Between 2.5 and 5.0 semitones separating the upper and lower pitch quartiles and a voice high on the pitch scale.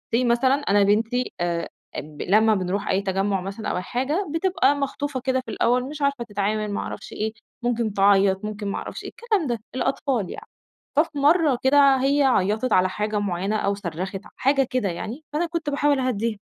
No: wide, 5.6 semitones; high, 230 Hz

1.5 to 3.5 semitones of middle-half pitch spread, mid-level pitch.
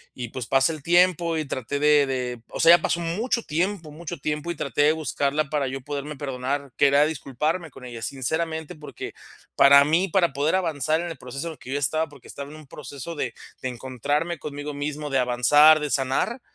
Yes: average, 3.0 semitones; medium, 145 Hz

